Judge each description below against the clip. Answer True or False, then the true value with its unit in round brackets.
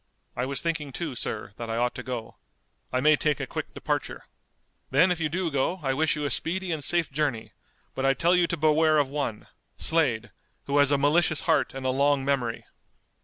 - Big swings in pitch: False (3.3 semitones)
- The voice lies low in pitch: False (145 Hz)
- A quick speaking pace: True (215 wpm)